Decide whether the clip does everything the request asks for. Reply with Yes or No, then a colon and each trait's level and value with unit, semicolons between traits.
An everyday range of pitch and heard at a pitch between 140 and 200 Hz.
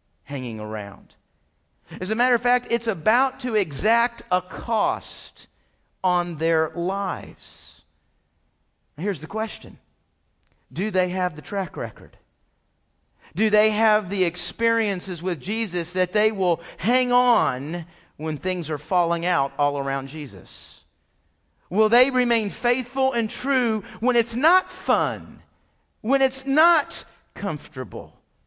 No: wide, 8.9 semitones; medium, 185 Hz